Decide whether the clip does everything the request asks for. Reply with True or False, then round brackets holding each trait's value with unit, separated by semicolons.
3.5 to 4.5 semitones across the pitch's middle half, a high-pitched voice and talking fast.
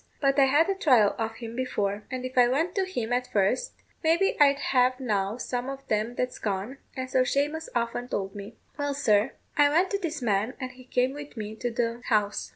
True (4.1 semitones; 250 Hz; 220 wpm)